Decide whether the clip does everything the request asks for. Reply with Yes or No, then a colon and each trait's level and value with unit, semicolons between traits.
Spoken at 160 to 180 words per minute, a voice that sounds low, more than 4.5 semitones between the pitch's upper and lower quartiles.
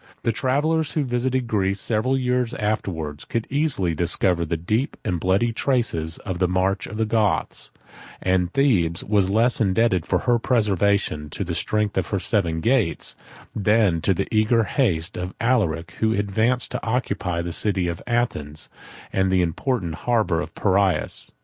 Yes: average, 165 wpm; low, 100 Hz; average, 4.9 semitones